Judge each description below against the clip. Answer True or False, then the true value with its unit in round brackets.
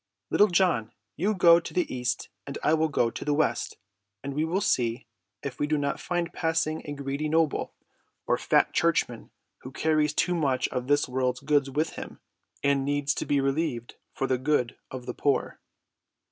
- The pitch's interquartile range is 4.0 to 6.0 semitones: False (3.4 semitones)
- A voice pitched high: False (145 Hz)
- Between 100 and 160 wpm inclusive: False (190 wpm)